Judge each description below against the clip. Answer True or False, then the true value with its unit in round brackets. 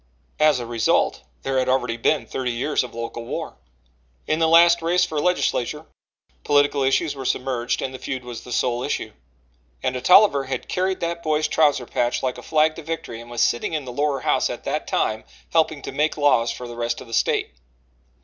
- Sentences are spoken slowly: False (205 wpm)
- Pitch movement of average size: True (4.2 semitones)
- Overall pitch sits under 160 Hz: True (135 Hz)